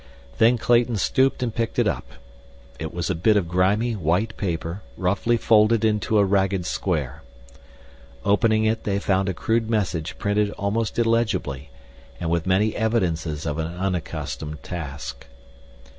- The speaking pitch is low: Yes, low, 100 Hz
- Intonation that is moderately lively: Yes, average, 4.7 semitones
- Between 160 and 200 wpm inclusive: No, average, 145 wpm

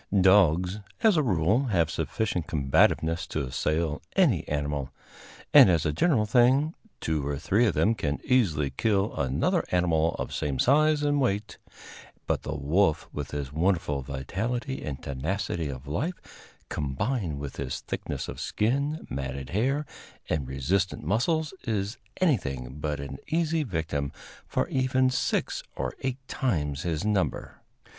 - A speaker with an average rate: Yes, average, 145 wpm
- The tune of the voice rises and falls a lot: Yes, wide, 9.0 semitones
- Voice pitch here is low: Yes, very low, 90 Hz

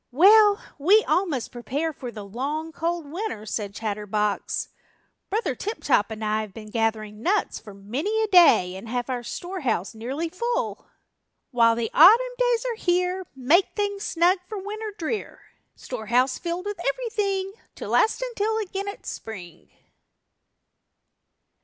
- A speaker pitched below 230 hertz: No, very high, 325 Hz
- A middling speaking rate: Yes, average, 145 wpm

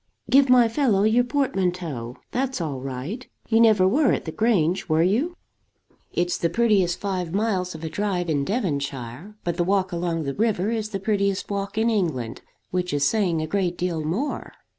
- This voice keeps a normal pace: Yes, average, 185 wpm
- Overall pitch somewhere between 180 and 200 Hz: Yes, medium, 185 Hz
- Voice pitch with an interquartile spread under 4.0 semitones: No, average, 5.1 semitones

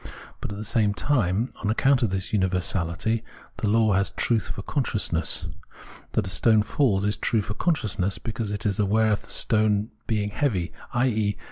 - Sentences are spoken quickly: No, average, 180 wpm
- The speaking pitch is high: No, low, 105 Hz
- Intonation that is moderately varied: No, narrow, 2.2 semitones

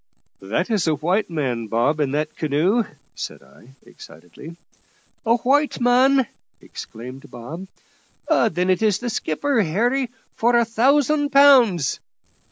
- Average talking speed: No, slow, 125 wpm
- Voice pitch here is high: Yes, high, 195 Hz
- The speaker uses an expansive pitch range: Yes, wide, 8.5 semitones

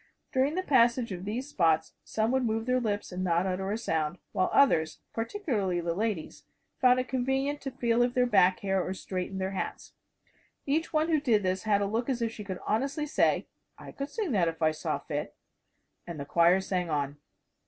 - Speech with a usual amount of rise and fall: No, wide, 5.7 semitones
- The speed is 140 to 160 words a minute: No, fast, 205 wpm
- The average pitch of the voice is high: Yes, high, 215 Hz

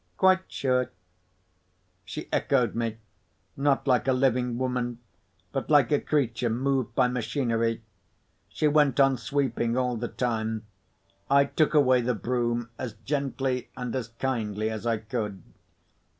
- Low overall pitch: Yes, low, 125 Hz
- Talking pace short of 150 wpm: Yes, slow, 135 wpm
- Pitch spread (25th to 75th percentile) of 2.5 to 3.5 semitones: Yes, average, 2.8 semitones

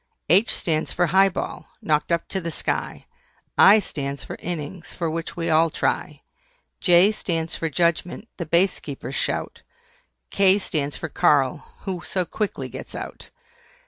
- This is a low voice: No, medium, 170 Hz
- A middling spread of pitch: Yes, average, 3.0 semitones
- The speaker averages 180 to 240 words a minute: No, average, 155 wpm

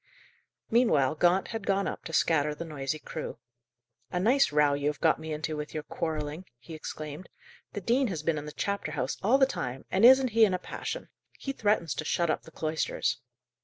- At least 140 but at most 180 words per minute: No, fast, 205 wpm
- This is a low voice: No, medium, 160 Hz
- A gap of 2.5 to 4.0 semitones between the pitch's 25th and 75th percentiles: No, average, 5.0 semitones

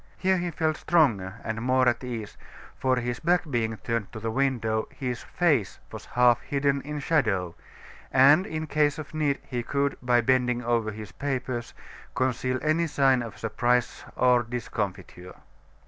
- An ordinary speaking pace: Yes, average, 160 wpm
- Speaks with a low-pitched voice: Yes, low, 125 Hz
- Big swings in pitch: No, average, 3.7 semitones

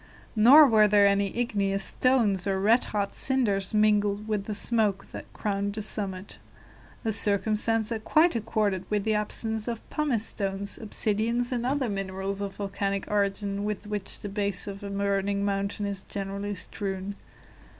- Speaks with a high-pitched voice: Yes, high, 205 Hz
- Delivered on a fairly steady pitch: Yes, narrow, 1.7 semitones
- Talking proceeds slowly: No, average, 160 wpm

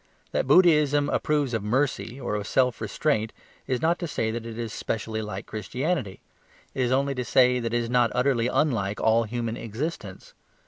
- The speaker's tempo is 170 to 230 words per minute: Yes, average, 185 wpm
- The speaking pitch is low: Yes, low, 120 Hz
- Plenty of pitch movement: No, average, 3.8 semitones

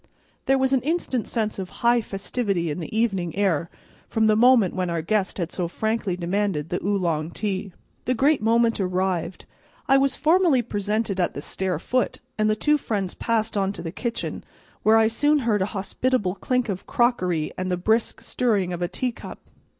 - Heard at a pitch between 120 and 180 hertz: No, high, 210 Hz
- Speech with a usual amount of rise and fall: Yes, average, 4.6 semitones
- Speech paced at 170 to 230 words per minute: Yes, average, 190 wpm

